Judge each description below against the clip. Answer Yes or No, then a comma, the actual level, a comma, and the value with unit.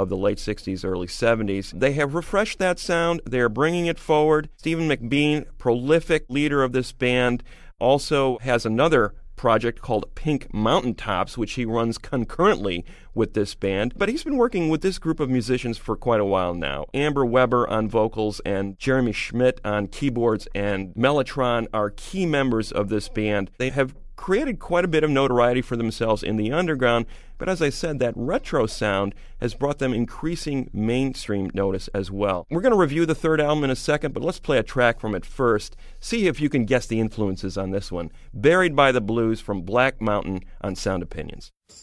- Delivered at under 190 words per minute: No, average, 195 wpm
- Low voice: Yes, low, 120 Hz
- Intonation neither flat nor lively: No, wide, 5.7 semitones